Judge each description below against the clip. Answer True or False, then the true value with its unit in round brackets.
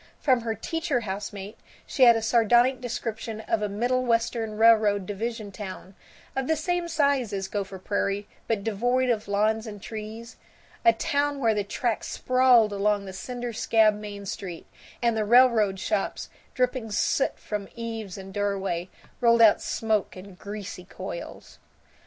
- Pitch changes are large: False (3.1 semitones)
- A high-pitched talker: True (220 Hz)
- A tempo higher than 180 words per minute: False (150 wpm)